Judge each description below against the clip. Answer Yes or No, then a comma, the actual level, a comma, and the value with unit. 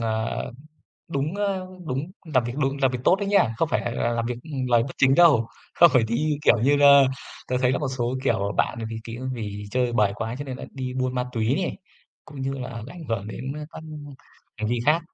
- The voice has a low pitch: Yes, low, 130 Hz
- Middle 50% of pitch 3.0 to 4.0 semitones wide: Yes, average, 3.6 semitones